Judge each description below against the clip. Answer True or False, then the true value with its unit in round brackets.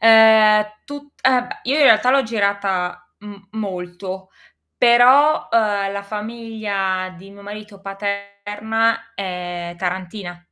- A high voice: True (205 Hz)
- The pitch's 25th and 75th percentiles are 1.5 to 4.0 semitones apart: True (2.9 semitones)